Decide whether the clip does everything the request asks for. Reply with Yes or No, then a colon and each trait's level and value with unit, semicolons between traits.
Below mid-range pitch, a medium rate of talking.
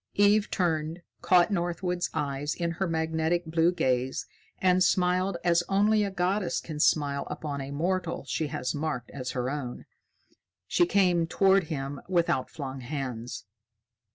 No: medium, 165 Hz; average, 145 wpm